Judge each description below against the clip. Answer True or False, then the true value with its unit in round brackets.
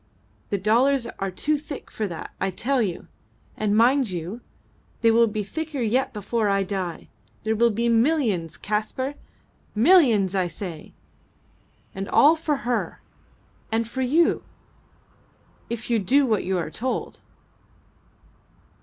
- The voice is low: False (225 Hz)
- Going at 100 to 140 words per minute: True (135 wpm)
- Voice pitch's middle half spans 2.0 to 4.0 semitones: False (4.8 semitones)